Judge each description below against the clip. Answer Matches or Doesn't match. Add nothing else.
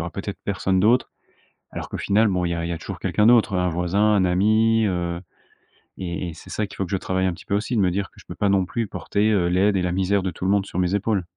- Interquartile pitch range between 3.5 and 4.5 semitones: Doesn't match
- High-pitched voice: Doesn't match